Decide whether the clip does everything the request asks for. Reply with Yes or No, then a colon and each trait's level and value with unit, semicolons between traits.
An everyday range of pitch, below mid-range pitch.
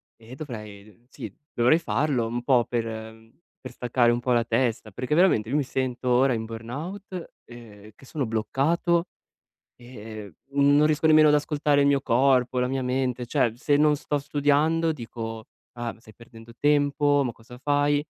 Yes: average, 3.9 semitones; low, 125 Hz